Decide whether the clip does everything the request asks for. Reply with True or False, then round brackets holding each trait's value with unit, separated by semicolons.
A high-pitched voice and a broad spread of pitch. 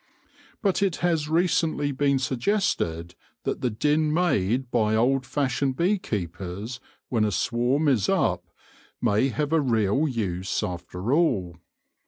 False (130 Hz; 6.4 semitones)